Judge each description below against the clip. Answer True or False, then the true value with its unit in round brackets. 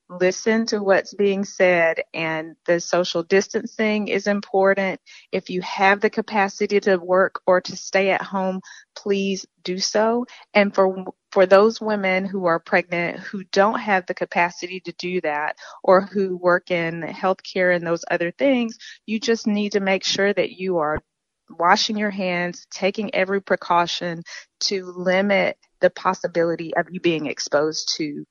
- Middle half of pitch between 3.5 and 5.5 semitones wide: False (2.4 semitones)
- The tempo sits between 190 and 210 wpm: False (160 wpm)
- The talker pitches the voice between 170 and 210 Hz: True (190 Hz)